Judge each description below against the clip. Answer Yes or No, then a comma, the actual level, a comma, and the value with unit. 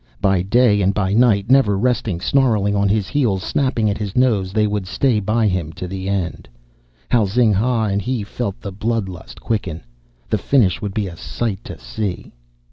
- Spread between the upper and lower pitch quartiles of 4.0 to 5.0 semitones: No, average, 3.4 semitones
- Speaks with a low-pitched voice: Yes, low, 105 Hz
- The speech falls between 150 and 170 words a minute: No, average, 195 wpm